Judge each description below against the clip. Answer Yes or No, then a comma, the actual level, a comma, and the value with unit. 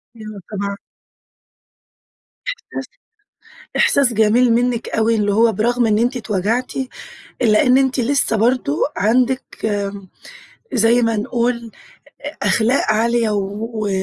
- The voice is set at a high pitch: Yes, high, 230 Hz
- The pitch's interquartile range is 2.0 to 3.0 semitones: Yes, narrow, 2.6 semitones